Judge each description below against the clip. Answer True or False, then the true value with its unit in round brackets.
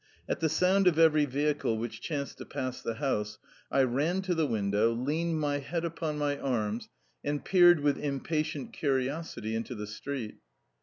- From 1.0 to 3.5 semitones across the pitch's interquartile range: False (5.1 semitones)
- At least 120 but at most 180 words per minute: True (170 wpm)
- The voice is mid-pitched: True (145 Hz)